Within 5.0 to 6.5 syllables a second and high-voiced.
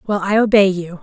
Yes: 5.5 syllables/s; high, 195 Hz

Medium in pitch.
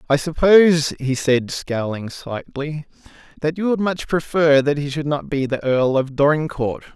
Yes: medium, 145 Hz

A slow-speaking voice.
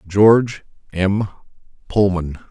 Yes: slow, 70 wpm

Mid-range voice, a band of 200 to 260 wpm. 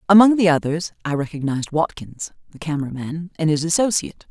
No: medium, 165 Hz; average, 165 wpm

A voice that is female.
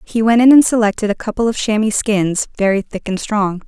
Yes: female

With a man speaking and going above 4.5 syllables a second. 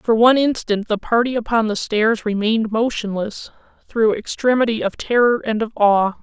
No: female; 5.0 syllables/s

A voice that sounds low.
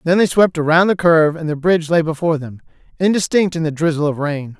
No: medium, 160 Hz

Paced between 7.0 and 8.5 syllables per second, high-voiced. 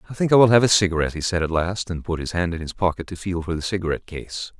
No: 7.1 syllables/s; very low, 90 Hz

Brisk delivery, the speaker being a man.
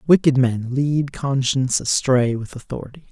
No: slow, 135 wpm; male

